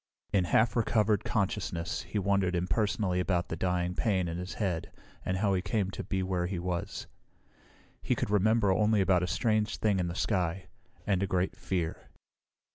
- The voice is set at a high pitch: No, very low, 95 Hz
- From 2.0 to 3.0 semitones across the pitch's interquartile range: Yes, narrow, 2.6 semitones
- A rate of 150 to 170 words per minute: No, average, 180 wpm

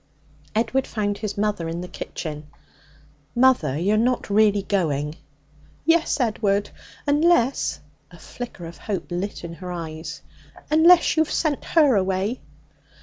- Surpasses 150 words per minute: No, slow, 135 wpm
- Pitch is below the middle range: No, high, 205 Hz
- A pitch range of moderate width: No, wide, 6.5 semitones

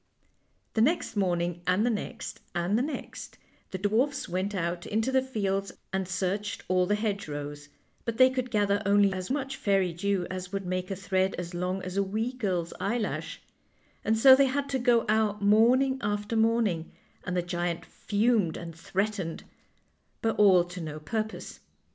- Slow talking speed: No, average, 170 wpm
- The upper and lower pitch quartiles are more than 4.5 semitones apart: No, average, 3.8 semitones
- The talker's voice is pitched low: No, high, 200 Hz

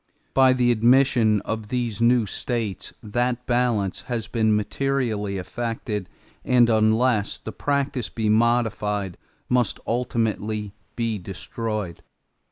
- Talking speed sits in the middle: No, slow, 110 wpm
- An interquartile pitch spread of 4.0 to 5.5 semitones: No, average, 2.7 semitones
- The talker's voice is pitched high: No, low, 115 Hz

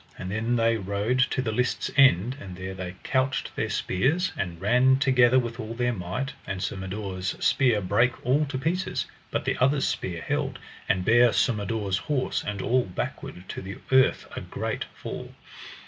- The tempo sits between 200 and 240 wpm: No, average, 180 wpm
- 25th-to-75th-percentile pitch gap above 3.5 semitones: Yes, average, 5.3 semitones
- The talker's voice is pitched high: No, low, 115 Hz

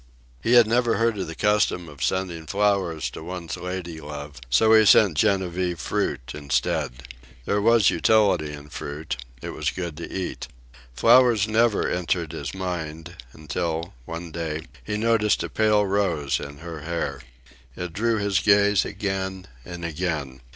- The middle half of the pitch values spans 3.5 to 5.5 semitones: Yes, average, 4.6 semitones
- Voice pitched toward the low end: Yes, very low, 90 Hz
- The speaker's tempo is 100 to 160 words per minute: Yes, average, 155 wpm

